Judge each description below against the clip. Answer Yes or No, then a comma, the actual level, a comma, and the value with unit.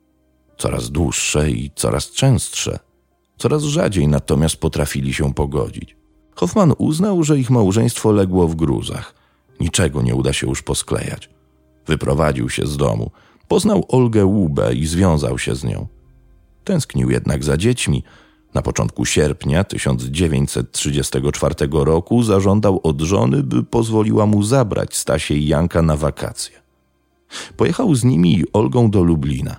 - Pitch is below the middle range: Yes, very low, 80 Hz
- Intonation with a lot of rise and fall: Yes, wide, 7.4 semitones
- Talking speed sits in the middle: Yes, average, 130 wpm